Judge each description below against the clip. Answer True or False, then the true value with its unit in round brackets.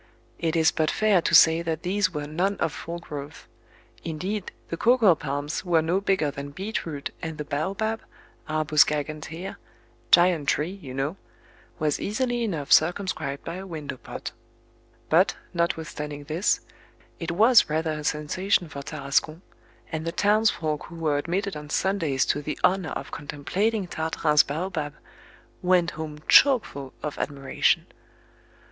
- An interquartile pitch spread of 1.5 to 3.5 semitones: False (3.9 semitones)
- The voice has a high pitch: False (160 Hz)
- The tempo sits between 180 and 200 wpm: False (145 wpm)